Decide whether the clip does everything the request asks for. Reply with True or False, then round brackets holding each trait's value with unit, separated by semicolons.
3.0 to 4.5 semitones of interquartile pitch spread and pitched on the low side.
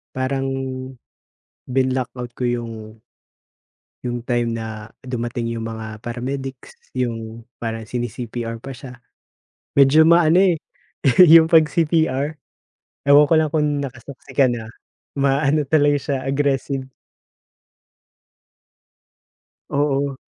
True (3.4 semitones; 130 Hz)